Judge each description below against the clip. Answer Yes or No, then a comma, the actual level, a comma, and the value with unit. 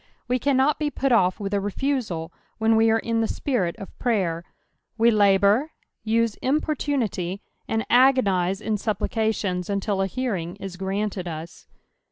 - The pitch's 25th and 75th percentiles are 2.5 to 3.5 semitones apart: No, average, 4.2 semitones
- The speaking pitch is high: Yes, high, 215 Hz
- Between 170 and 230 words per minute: No, average, 155 wpm